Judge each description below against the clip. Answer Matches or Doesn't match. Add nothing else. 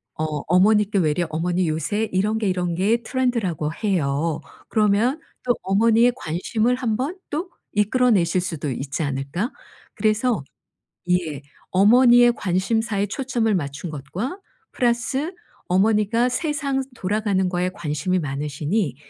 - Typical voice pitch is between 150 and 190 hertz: Doesn't match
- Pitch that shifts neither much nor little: Doesn't match